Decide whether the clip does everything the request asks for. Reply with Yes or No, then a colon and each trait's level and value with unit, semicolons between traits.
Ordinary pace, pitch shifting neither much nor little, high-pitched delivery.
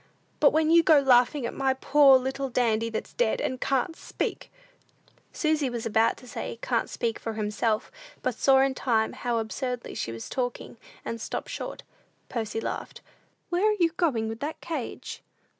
Yes: average, 180 wpm; average, 4.3 semitones; very high, 255 Hz